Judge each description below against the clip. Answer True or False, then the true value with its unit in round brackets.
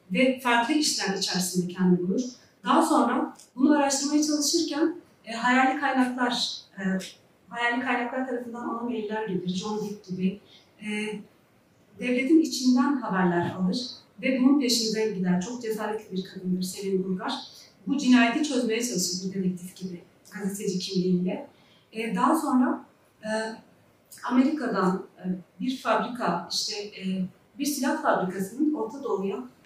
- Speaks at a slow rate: False (125 wpm)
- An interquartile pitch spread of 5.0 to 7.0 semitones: True (5.5 semitones)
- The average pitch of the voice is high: True (220 Hz)